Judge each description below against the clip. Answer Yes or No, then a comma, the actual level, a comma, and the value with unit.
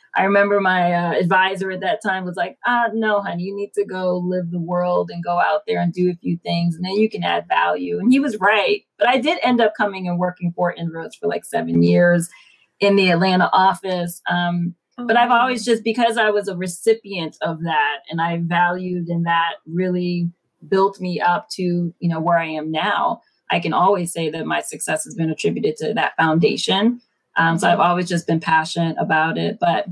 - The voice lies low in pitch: No, medium, 180 Hz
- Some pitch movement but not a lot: Yes, average, 3.1 semitones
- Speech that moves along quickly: Yes, fast, 215 wpm